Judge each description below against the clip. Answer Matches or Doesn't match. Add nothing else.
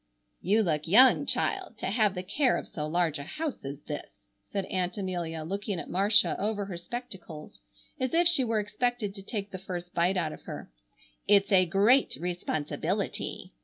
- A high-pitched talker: Matches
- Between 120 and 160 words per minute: Doesn't match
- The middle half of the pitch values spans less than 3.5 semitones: Doesn't match